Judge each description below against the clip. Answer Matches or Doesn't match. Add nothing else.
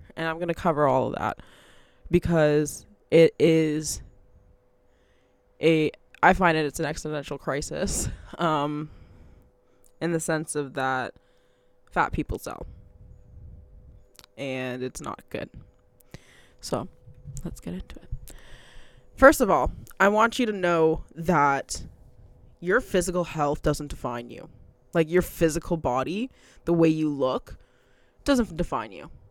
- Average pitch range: Doesn't match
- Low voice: Doesn't match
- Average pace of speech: Doesn't match